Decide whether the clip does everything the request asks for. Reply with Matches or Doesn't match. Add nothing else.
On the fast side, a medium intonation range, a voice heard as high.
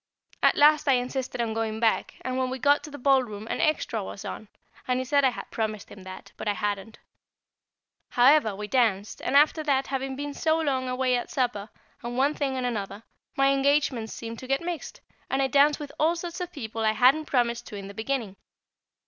Matches